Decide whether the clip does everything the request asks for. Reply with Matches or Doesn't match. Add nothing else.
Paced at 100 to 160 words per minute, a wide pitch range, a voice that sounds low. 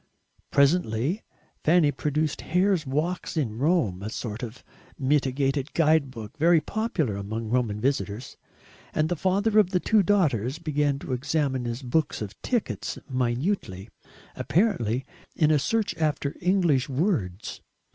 Doesn't match